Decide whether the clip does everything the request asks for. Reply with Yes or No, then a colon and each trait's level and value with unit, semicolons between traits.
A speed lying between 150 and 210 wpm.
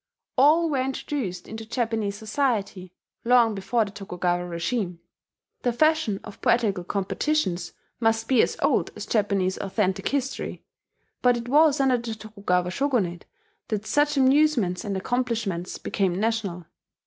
No: slow, 135 wpm